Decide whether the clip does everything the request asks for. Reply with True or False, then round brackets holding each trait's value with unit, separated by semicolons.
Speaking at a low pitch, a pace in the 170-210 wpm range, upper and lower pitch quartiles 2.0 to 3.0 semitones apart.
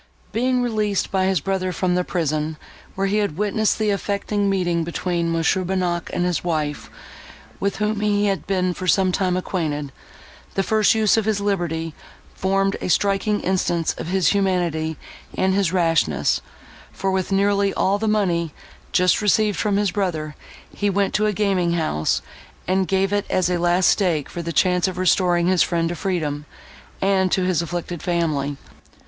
False (185 Hz; 175 wpm; 2.7 semitones)